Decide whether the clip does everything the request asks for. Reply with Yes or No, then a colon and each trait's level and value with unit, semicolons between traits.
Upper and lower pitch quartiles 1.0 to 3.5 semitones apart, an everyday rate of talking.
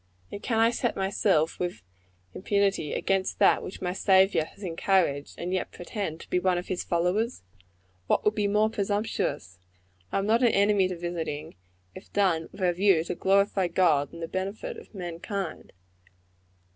Yes: average, 2.9 semitones; average, 170 wpm